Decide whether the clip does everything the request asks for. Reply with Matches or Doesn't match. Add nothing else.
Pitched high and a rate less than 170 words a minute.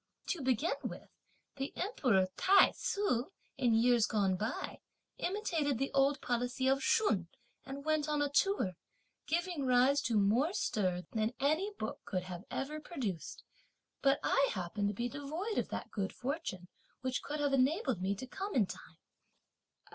Matches